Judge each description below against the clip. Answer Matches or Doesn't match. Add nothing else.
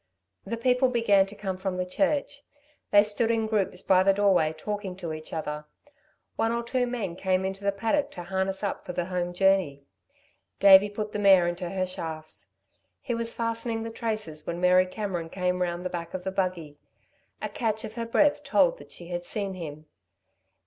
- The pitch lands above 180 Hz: Matches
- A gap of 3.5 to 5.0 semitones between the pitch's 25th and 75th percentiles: Matches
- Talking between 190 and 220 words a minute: Matches